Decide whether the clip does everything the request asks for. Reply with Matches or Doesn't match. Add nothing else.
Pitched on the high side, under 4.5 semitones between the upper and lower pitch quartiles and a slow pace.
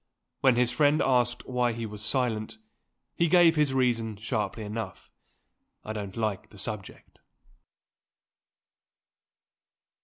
Doesn't match